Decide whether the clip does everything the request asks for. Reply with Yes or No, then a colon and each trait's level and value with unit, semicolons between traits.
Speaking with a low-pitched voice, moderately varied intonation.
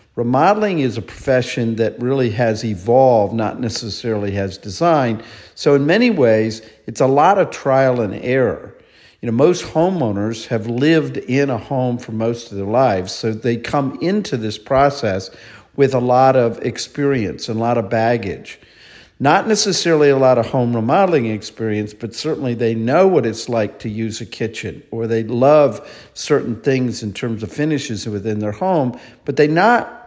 Yes: low, 120 Hz; average, 3.8 semitones